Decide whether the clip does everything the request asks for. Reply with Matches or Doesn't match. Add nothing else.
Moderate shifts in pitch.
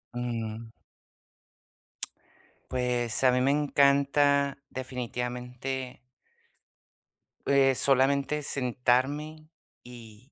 Doesn't match